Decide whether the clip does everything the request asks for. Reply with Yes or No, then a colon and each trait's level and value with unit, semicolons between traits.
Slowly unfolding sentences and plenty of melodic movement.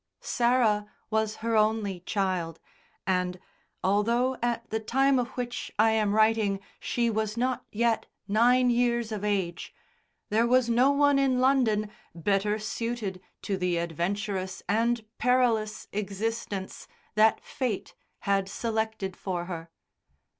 No: slow, 125 wpm; average, 3.2 semitones